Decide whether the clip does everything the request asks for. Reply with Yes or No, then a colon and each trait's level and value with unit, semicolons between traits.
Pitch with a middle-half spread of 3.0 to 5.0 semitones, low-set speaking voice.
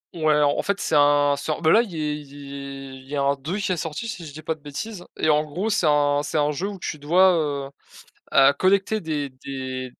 No: average, 3.3 semitones; medium, 150 Hz